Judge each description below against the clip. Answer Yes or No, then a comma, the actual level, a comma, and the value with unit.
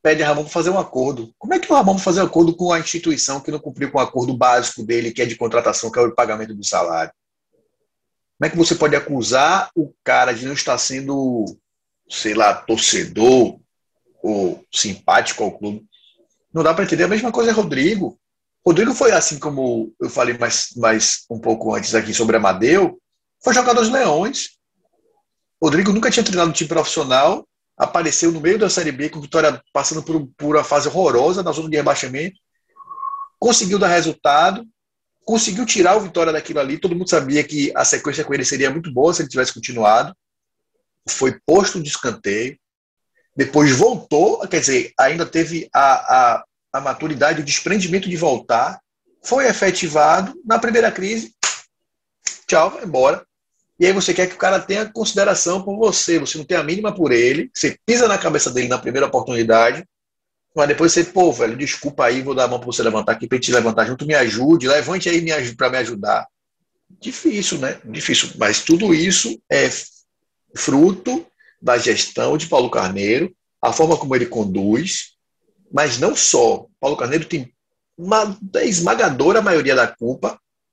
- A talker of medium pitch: Yes, medium, 160 Hz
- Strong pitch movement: Yes, wide, 6.8 semitones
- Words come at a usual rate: Yes, average, 175 wpm